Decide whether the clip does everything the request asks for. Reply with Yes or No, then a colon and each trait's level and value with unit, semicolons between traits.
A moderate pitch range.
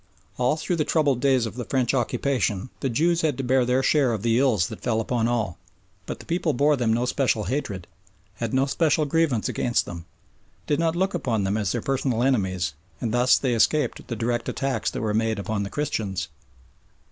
Yes: average, 4.0 semitones